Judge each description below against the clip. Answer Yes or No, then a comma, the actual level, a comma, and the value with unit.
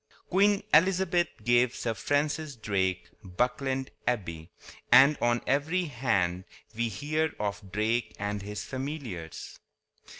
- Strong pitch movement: Yes, wide, 6.4 semitones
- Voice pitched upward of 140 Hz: No, low, 120 Hz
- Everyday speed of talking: No, slow, 110 wpm